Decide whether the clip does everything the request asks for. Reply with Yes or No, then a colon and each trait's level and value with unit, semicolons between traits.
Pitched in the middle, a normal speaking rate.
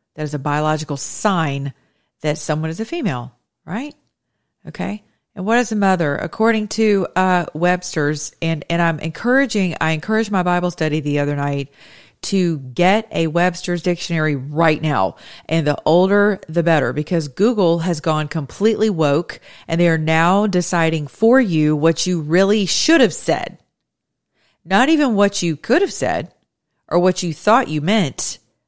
Yes: medium, 170 Hz; average, 160 wpm